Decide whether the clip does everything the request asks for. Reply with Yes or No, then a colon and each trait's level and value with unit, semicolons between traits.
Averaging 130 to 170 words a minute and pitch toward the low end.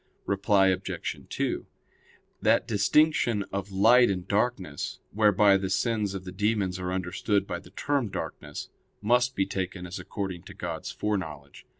Yes: average, 150 wpm; low, 100 Hz